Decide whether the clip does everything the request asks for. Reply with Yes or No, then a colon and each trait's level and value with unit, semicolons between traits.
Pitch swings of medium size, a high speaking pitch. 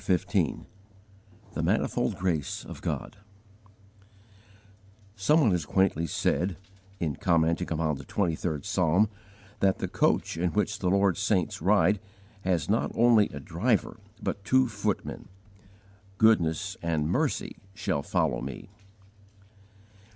No: average, 3.8 semitones; very low, 95 Hz